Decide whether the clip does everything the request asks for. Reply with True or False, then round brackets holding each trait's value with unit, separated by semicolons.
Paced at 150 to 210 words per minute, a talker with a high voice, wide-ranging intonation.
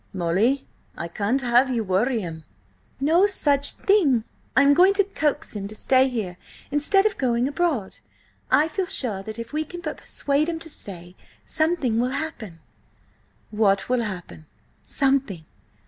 True (160 wpm; 255 Hz; 6.8 semitones)